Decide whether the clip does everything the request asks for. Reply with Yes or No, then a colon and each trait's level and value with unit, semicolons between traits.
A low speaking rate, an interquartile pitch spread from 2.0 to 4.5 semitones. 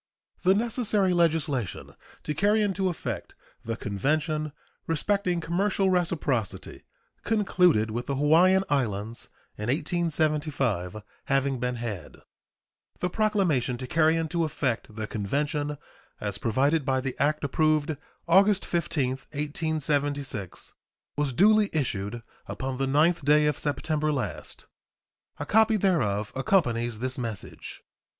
No: slow, 115 wpm; wide, 5.5 semitones